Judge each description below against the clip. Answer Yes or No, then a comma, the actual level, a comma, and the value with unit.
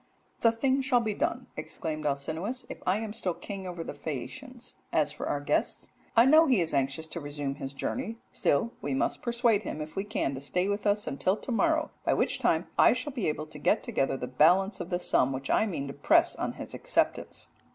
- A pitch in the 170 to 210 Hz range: Yes, high, 190 Hz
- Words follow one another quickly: Yes, fast, 225 wpm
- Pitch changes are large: Yes, wide, 8.3 semitones